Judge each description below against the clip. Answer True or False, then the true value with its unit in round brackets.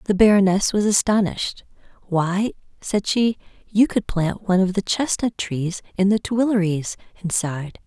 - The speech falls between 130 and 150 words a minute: True (145 wpm)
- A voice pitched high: True (195 Hz)